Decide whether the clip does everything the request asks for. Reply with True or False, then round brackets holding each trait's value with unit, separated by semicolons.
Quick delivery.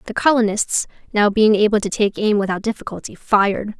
False (175 wpm)